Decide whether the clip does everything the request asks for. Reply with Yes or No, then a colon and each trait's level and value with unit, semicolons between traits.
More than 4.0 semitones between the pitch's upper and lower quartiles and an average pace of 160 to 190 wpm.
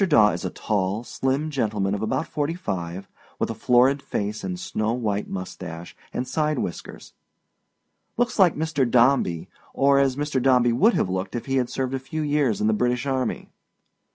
Yes: wide, 5.4 semitones; average, 180 wpm